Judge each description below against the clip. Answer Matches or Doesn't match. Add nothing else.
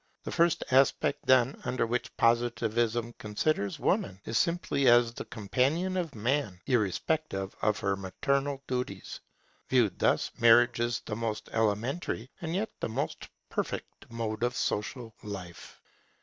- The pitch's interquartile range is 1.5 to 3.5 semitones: Doesn't match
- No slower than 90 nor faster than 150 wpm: Matches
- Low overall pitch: Matches